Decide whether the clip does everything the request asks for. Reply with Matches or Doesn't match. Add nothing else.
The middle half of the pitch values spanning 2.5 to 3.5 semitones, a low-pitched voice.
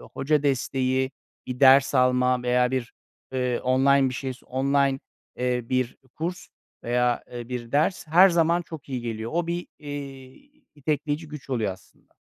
Matches